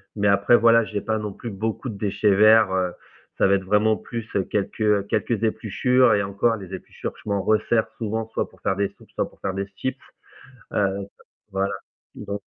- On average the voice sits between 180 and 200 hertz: No, low, 105 Hz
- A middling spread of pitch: No, narrow, 2.1 semitones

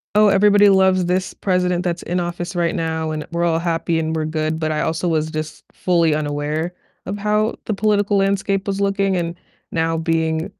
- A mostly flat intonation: No, average, 3.3 semitones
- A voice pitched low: No, medium, 175 Hz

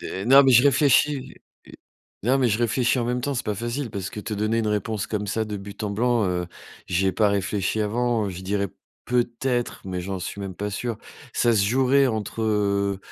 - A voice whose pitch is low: Yes, low, 110 Hz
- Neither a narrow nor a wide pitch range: Yes, average, 3.4 semitones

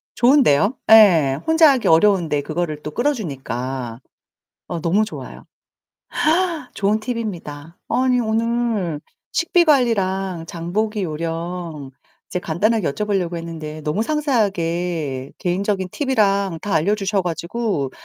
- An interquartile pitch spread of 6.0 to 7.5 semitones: No, average, 5.3 semitones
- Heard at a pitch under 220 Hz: Yes, medium, 185 Hz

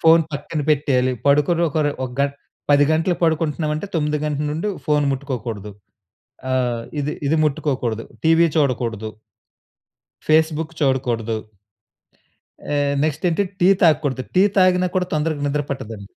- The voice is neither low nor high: Yes, medium, 150 Hz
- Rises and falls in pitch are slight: No, average, 3.7 semitones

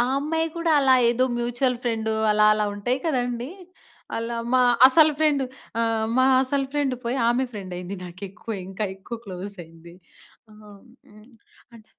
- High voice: Yes, high, 235 Hz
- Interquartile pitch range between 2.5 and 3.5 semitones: No, average, 4.4 semitones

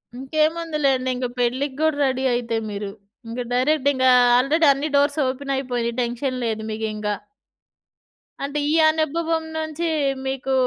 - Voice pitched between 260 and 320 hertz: Yes, very high, 265 Hz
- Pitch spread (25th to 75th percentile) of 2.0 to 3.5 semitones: No, average, 3.9 semitones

